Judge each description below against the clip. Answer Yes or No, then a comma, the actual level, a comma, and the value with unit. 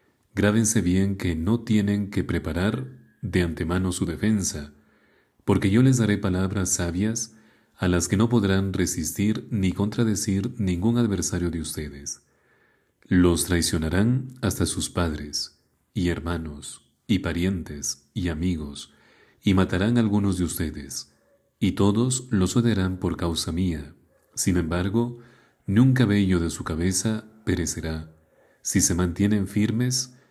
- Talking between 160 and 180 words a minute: No, average, 130 wpm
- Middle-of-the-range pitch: No, very low, 95 Hz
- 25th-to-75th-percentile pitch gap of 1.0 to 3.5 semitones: No, average, 4.1 semitones